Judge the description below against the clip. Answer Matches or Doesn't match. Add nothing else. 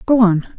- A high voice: Matches